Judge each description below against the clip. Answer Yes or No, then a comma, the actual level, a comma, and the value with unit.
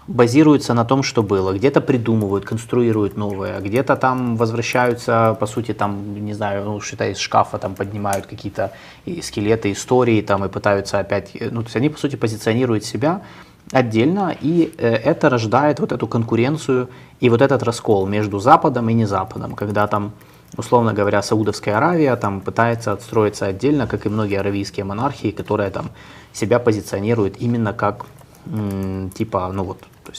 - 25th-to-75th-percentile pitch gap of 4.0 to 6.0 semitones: No, average, 3.4 semitones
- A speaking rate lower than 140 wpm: No, average, 155 wpm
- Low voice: Yes, low, 110 Hz